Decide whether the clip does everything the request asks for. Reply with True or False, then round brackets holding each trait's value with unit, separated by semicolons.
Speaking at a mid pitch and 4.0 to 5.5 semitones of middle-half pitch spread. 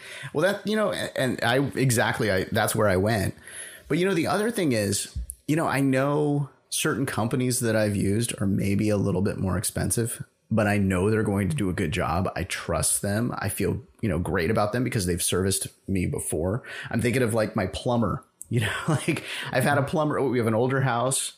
False (115 Hz; 4.9 semitones)